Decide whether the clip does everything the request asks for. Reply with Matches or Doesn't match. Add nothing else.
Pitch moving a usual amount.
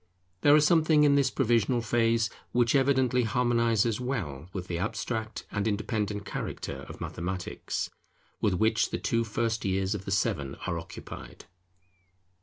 Matches